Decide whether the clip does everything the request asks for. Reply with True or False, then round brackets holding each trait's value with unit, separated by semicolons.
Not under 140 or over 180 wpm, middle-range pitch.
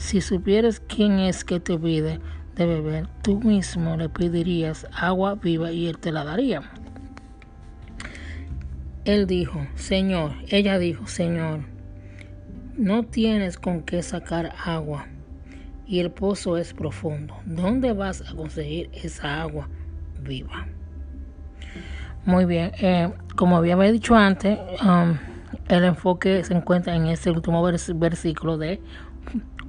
False (125 wpm; 170 Hz)